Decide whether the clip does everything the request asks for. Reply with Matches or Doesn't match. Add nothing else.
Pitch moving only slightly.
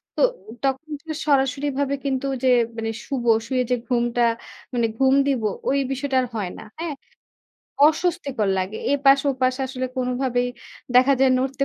Matches